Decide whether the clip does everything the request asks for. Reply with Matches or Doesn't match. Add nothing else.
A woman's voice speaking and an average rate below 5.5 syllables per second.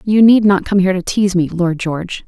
Doesn't match